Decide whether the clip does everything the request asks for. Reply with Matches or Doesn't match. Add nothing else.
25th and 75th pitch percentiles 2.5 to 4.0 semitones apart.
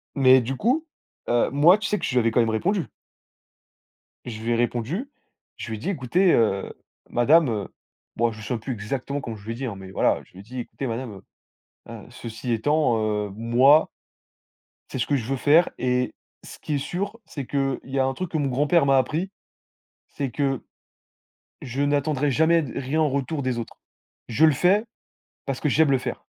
Doesn't match